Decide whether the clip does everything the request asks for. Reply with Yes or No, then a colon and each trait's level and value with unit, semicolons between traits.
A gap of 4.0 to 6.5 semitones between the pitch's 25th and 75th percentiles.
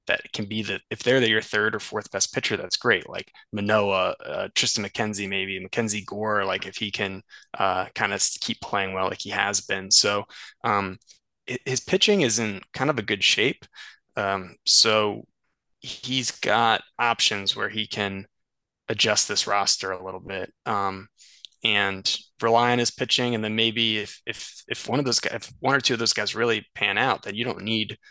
No: average, 2.9 semitones